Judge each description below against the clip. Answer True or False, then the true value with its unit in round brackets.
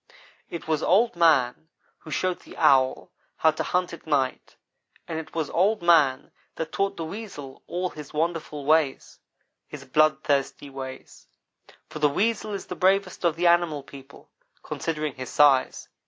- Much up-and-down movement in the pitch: False (3.6 semitones)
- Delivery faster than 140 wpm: True (155 wpm)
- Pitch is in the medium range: True (160 Hz)